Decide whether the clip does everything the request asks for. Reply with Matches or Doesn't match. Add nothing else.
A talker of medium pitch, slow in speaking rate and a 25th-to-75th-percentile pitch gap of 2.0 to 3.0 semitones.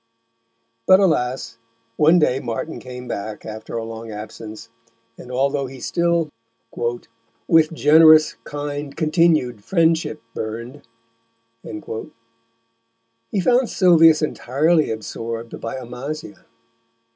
Doesn't match